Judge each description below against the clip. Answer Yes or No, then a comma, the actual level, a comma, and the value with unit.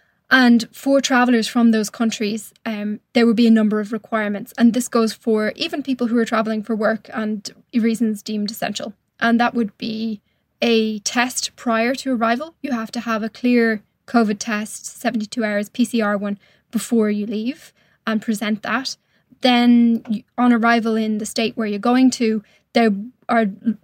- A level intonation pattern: Yes, narrow, 1.9 semitones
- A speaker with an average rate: Yes, average, 170 wpm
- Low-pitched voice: No, high, 225 Hz